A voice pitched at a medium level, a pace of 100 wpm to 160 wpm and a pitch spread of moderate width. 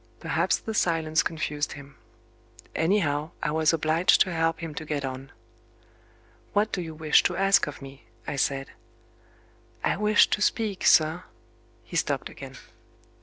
Yes: medium, 155 Hz; average, 155 wpm; average, 3.7 semitones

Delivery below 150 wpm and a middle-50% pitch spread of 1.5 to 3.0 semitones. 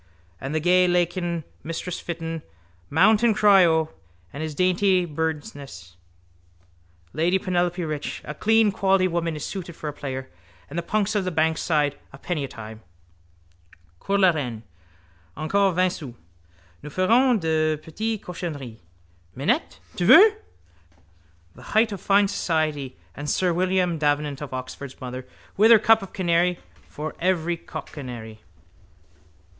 No: average, 140 wpm; average, 4.2 semitones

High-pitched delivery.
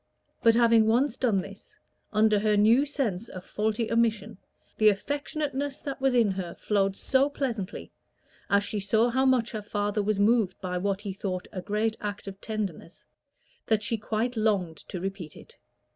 Yes: high, 215 Hz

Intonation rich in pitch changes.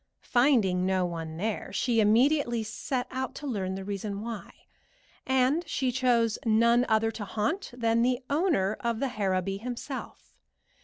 No: average, 4.0 semitones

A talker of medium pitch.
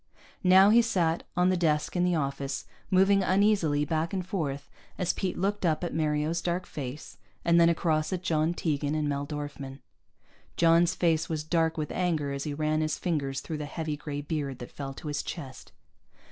Yes: medium, 160 Hz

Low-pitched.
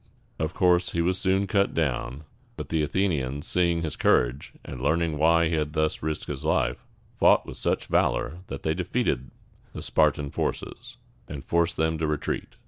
Yes: very low, 80 Hz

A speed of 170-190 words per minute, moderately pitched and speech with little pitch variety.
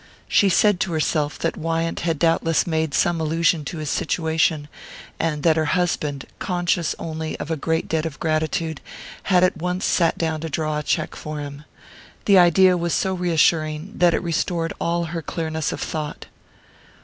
Yes: average, 175 wpm; medium, 165 Hz; narrow, 1.9 semitones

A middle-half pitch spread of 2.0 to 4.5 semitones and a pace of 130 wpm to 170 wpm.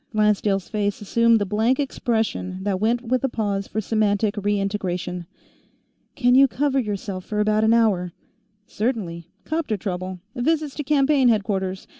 Yes: average, 3.7 semitones; average, 150 wpm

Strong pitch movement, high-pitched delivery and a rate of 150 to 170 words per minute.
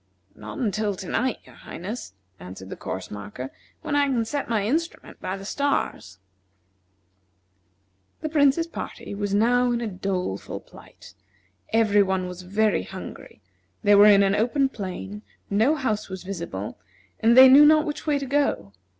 Yes: wide, 6.0 semitones; high, 210 Hz; average, 160 wpm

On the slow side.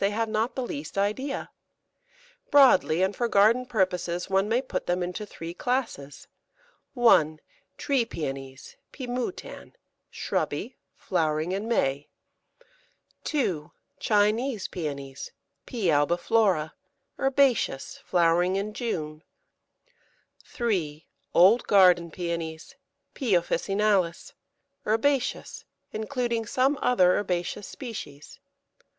Yes: slow, 100 wpm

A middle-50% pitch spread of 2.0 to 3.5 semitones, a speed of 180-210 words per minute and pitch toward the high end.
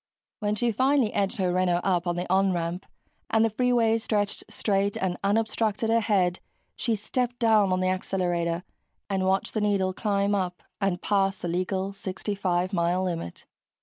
No: narrow, 2.6 semitones; average, 165 wpm; high, 195 Hz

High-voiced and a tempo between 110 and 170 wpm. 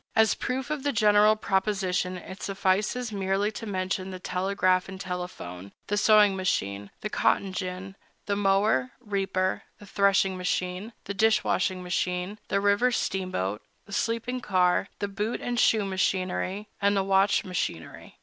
Yes: high, 195 Hz; average, 150 wpm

